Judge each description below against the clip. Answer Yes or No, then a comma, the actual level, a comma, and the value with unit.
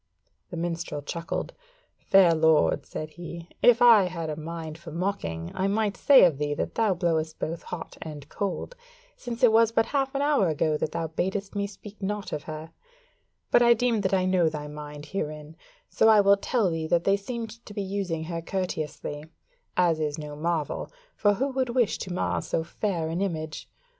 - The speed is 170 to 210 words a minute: Yes, average, 195 wpm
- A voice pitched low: No, medium, 175 Hz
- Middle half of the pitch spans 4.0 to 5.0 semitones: Yes, average, 4.6 semitones